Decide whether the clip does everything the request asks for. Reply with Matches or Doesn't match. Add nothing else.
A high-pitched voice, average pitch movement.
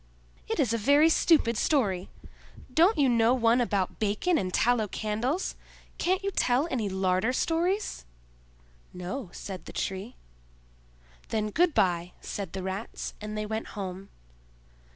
Doesn't match